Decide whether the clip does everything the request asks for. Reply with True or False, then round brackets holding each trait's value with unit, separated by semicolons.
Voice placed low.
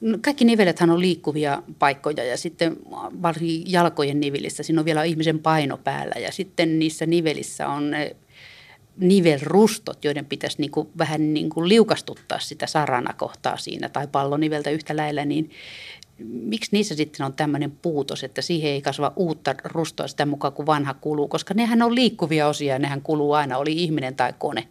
False (155 Hz)